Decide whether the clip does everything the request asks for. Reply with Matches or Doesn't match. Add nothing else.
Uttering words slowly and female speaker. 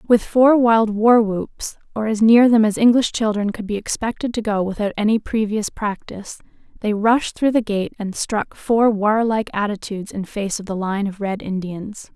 Doesn't match